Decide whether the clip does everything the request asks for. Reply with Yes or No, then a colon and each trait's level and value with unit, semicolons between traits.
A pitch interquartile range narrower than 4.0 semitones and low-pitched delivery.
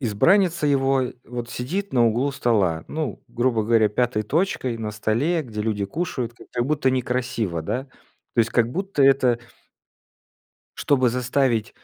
Yes: average, 3.4 semitones; low, 125 Hz